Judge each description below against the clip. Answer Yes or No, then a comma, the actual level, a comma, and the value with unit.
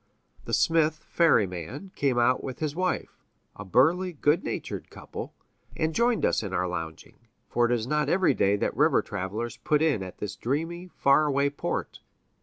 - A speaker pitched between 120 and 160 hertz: Yes, medium, 140 Hz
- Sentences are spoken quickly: No, average, 175 wpm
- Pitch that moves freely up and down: Yes, wide, 7.2 semitones